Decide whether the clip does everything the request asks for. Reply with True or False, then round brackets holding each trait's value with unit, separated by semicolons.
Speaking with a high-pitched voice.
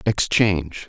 False (95 Hz)